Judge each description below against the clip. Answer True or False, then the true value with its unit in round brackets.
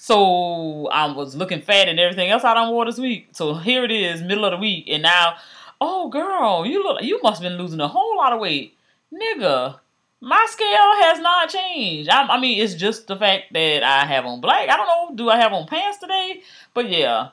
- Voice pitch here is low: False (220 Hz)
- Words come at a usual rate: False (230 wpm)